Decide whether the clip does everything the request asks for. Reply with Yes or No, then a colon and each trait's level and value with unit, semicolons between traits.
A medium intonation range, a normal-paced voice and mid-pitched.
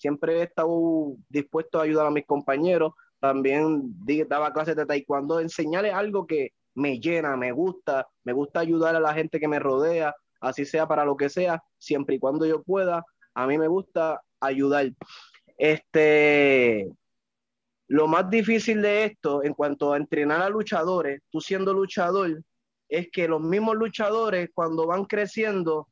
Yes: average, 3.6 semitones; average, 160 wpm; medium, 160 Hz